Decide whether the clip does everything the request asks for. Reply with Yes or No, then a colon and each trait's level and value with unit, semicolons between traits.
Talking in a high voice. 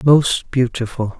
No: low, 125 Hz